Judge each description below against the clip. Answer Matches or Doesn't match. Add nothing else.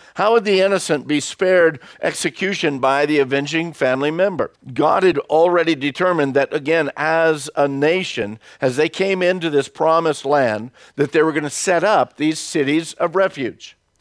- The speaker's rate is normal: Matches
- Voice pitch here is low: Doesn't match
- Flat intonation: Doesn't match